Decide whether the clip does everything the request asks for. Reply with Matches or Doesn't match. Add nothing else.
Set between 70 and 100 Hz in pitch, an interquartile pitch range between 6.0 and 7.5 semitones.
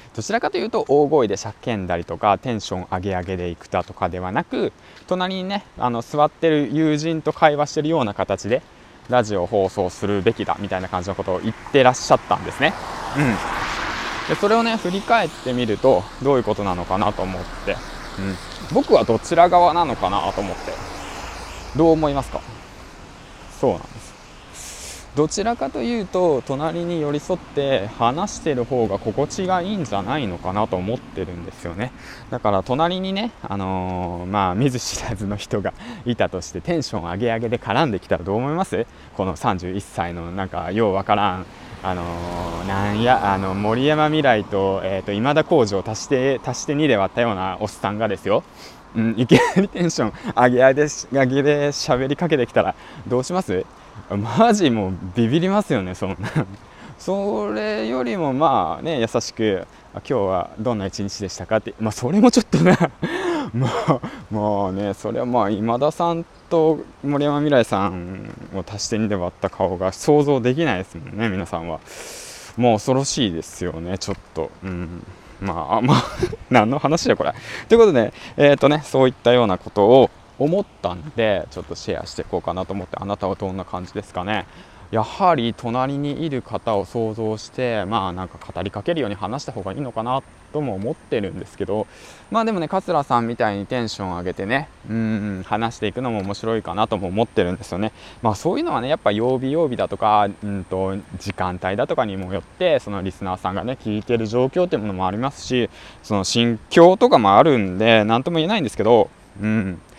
Doesn't match